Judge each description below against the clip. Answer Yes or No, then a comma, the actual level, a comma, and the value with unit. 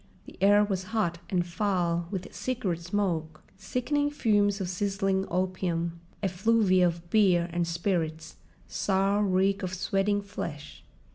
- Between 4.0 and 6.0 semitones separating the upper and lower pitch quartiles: No, average, 2.8 semitones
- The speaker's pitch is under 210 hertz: Yes, high, 190 Hz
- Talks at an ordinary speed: No, slow, 130 wpm